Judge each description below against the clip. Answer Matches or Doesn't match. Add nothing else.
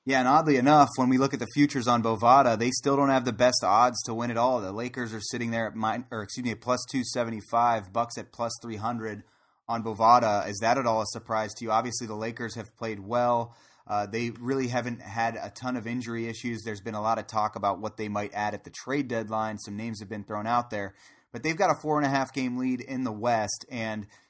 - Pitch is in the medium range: Doesn't match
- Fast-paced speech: Matches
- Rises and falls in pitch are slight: Matches